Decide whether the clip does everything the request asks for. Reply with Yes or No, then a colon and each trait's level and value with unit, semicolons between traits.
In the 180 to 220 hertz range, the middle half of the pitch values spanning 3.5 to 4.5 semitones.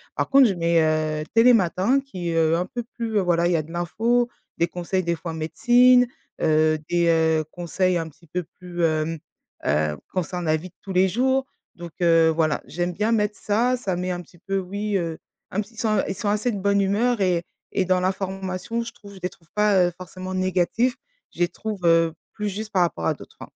Yes: medium, 185 Hz; average, 3.8 semitones